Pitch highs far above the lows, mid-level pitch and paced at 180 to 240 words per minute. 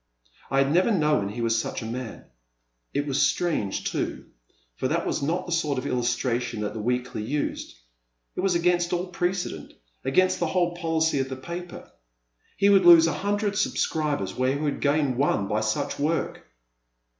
Yes: wide, 6.0 semitones; medium, 145 Hz; average, 190 wpm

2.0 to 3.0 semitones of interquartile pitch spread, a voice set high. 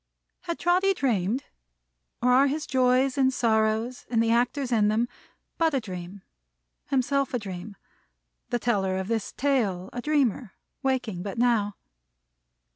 No: average, 4.4 semitones; high, 240 Hz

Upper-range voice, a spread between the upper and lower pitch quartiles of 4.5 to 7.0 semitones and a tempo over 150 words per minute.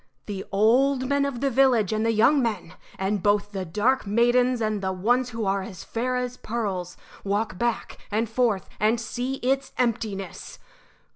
No: high, 225 Hz; average, 3.6 semitones; average, 170 wpm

